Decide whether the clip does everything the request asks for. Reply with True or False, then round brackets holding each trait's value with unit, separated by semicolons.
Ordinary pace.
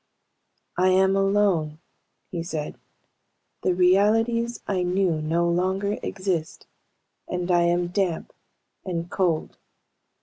False (105 wpm)